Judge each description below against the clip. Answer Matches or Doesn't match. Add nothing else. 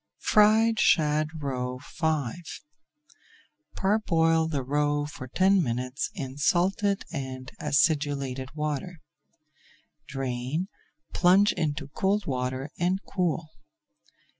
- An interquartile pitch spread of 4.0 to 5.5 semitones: Matches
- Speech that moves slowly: Matches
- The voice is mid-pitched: Matches